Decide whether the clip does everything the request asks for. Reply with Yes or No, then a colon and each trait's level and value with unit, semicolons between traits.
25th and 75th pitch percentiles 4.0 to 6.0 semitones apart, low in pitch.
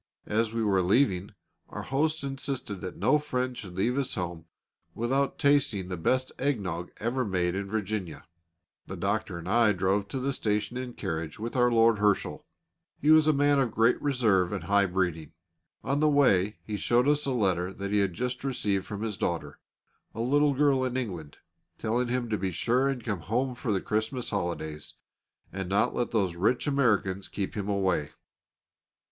Yes: average, 5.2 semitones; low, 110 Hz